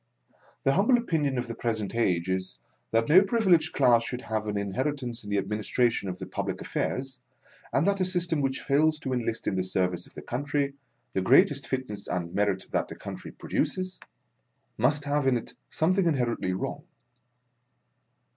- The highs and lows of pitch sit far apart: Yes, wide, 6.2 semitones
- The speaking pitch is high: No, low, 125 Hz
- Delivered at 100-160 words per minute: No, average, 180 wpm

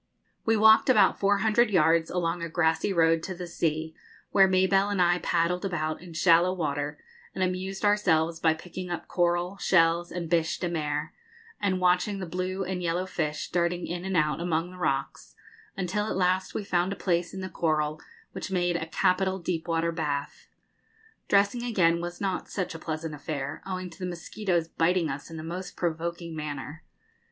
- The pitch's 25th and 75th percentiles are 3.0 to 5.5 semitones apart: No, narrow, 2.5 semitones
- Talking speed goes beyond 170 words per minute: Yes, average, 185 wpm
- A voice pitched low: No, medium, 175 Hz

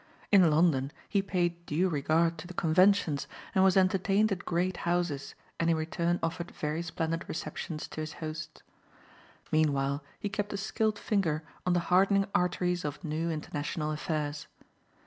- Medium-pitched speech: Yes, medium, 170 Hz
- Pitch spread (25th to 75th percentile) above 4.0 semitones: No, average, 3.1 semitones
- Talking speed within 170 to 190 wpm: No, average, 155 wpm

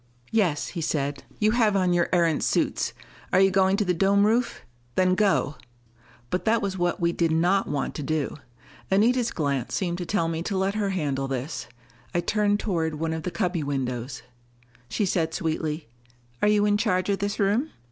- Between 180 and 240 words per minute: Yes, average, 190 wpm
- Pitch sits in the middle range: Yes, medium, 180 Hz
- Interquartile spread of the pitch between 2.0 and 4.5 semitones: Yes, average, 4.1 semitones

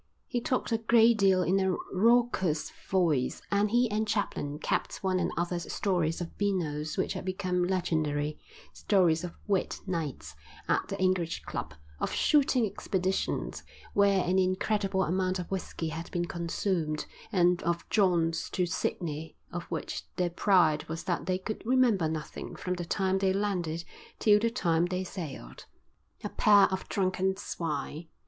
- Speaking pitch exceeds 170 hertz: Yes, medium, 185 Hz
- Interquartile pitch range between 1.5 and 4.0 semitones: Yes, average, 3.1 semitones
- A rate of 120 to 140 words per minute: No, average, 155 wpm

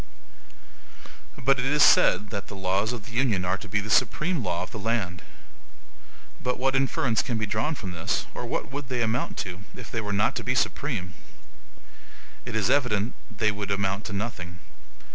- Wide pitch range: No, average, 4.1 semitones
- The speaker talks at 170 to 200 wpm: Yes, average, 190 wpm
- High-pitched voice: No, low, 110 Hz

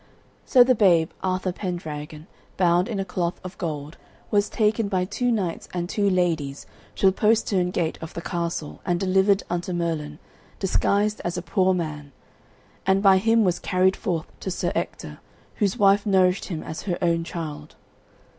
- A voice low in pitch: No, medium, 185 Hz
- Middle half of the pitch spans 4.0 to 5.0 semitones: No, average, 2.7 semitones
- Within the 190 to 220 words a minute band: No, average, 170 wpm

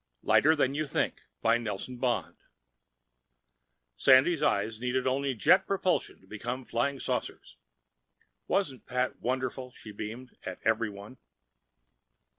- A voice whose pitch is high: No, low, 125 Hz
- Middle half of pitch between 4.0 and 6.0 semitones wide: No, average, 3.2 semitones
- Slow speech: Yes, slow, 115 wpm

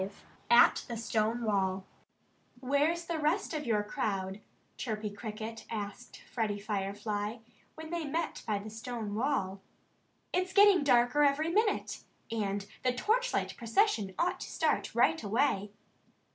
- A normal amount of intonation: No, wide, 6.7 semitones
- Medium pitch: No, high, 230 Hz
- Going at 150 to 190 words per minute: No, slow, 135 wpm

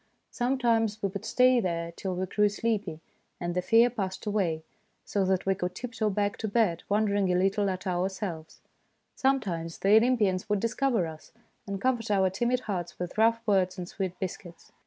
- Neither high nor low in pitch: No, high, 200 Hz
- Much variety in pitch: No, average, 3.6 semitones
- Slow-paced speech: No, average, 180 wpm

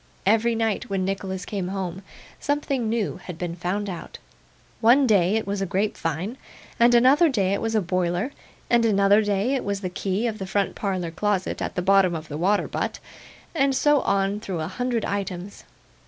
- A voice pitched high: Yes, high, 200 Hz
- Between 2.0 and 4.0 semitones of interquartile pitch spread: Yes, average, 3.3 semitones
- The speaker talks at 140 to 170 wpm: No, average, 190 wpm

